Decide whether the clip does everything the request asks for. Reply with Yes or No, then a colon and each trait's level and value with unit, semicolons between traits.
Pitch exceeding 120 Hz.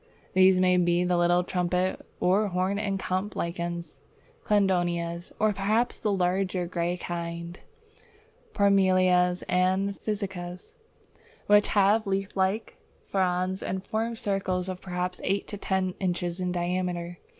Yes: medium, 185 Hz